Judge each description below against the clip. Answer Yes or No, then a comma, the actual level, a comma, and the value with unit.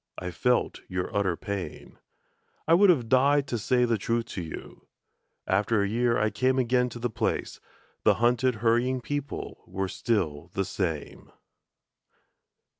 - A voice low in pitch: Yes, low, 115 Hz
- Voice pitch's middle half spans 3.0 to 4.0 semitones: No, average, 4.5 semitones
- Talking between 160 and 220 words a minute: No, average, 150 wpm